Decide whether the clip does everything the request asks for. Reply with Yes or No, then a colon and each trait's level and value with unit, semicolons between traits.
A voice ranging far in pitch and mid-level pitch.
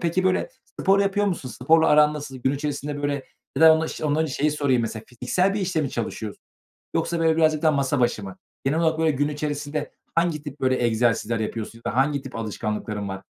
No: average, 4.5 semitones; medium, 145 Hz